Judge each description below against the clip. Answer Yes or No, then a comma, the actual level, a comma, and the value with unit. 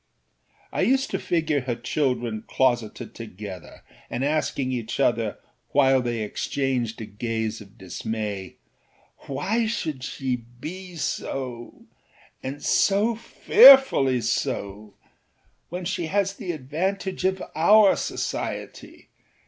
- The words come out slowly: Yes, slow, 105 wpm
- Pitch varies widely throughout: Yes, wide, 8.1 semitones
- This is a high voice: No, low, 135 Hz